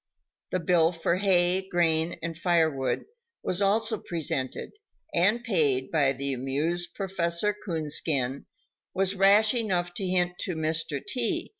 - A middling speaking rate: No, slow, 130 wpm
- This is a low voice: No, medium, 175 Hz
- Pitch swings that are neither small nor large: Yes, average, 3.4 semitones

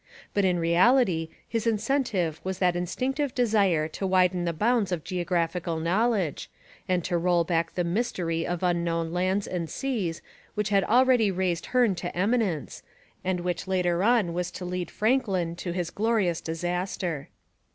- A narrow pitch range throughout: No, average, 3.6 semitones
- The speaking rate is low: No, average, 155 wpm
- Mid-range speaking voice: Yes, medium, 180 Hz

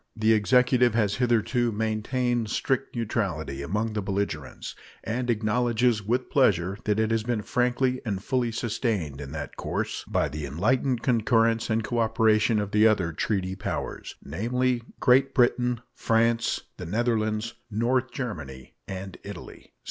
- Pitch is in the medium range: No, low, 110 Hz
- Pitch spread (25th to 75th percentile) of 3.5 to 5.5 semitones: No, average, 3.1 semitones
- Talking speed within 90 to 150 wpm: Yes, average, 140 wpm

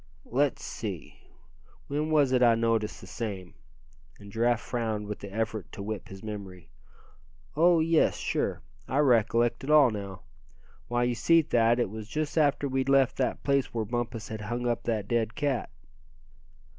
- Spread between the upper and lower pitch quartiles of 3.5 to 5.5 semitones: Yes, average, 4.1 semitones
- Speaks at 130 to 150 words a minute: No, average, 170 wpm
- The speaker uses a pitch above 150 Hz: No, low, 120 Hz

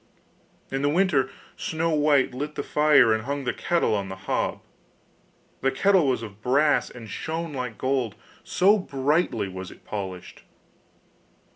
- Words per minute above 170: No, average, 150 wpm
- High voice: No, low, 135 Hz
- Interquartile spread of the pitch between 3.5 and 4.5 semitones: No, average, 5.3 semitones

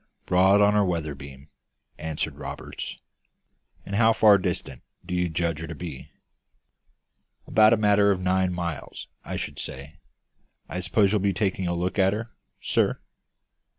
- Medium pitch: No, very low, 90 Hz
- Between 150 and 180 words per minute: Yes, average, 155 wpm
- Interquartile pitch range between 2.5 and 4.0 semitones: Yes, average, 3.7 semitones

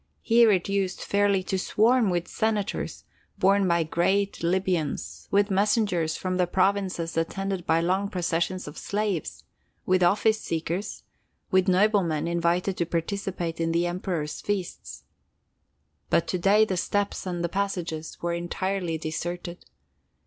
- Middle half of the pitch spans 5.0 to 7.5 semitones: No, average, 2.7 semitones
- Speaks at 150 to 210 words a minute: No, slow, 135 wpm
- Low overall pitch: No, medium, 185 Hz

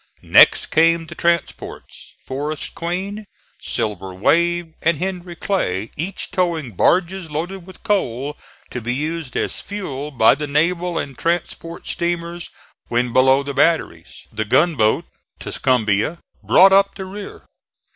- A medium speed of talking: No, slow, 130 wpm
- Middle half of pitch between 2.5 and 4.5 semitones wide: No, average, 5.1 semitones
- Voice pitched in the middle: Yes, medium, 165 Hz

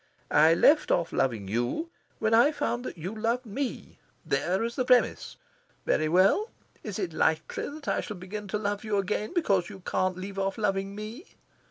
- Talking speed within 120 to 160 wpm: No, average, 185 wpm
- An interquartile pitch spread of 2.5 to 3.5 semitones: No, average, 4.1 semitones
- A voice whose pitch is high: Yes, high, 205 Hz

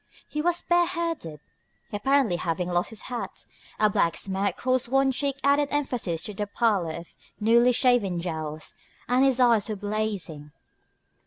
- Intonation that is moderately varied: No, wide, 6.9 semitones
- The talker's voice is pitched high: Yes, high, 220 Hz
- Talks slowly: No, average, 150 wpm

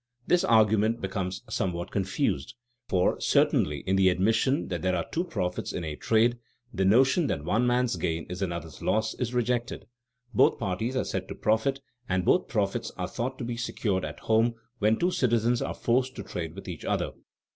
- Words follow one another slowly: No, average, 190 wpm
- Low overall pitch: Yes, low, 110 Hz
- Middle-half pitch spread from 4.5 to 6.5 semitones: Yes, average, 4.8 semitones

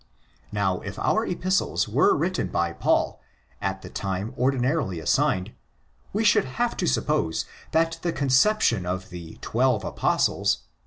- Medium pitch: No, low, 125 Hz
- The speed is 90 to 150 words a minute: Yes, average, 140 wpm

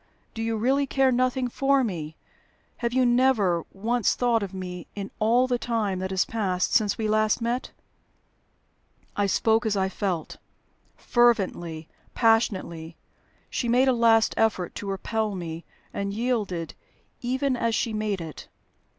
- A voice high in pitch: Yes, high, 220 Hz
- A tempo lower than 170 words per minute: Yes, average, 150 wpm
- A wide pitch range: No, average, 4.2 semitones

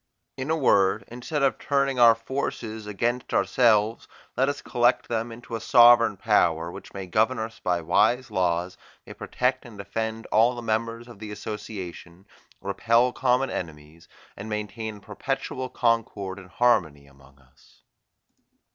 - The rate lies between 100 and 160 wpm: Yes, average, 150 wpm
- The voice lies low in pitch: Yes, low, 110 Hz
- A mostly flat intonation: No, average, 3.8 semitones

